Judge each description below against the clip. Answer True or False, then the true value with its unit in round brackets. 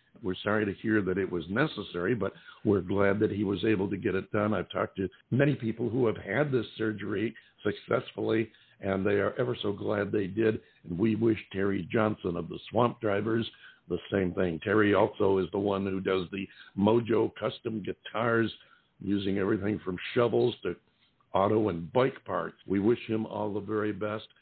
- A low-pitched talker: True (105 Hz)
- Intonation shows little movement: True (2.0 semitones)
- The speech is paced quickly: False (190 wpm)